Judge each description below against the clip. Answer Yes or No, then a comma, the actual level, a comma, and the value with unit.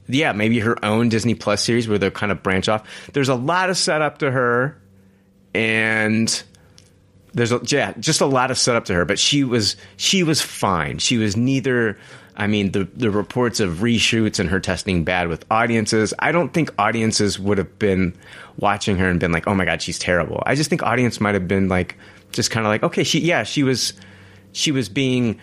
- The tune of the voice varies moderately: Yes, average, 4.2 semitones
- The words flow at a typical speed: No, fast, 210 wpm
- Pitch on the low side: Yes, low, 110 Hz